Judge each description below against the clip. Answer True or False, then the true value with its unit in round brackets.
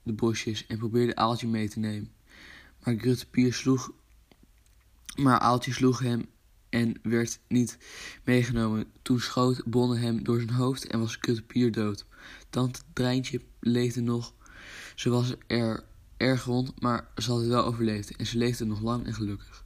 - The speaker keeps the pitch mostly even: True (1.6 semitones)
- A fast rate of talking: False (155 wpm)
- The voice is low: True (120 Hz)